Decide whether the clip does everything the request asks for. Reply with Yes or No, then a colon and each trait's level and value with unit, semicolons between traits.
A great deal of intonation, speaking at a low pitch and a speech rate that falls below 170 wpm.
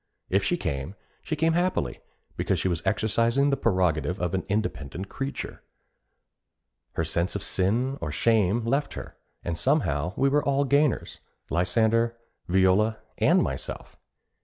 Yes: wide, 7.4 semitones; low, 105 Hz; average, 140 wpm